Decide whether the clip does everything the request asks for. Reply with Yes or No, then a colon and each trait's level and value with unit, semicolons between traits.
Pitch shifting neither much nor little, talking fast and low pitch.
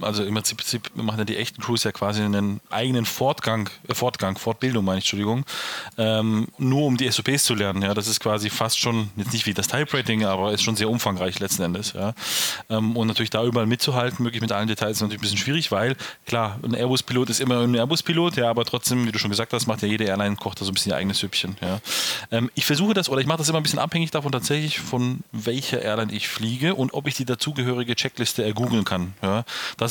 Yes: average, 3.0 semitones; fast, 240 wpm; low, 115 Hz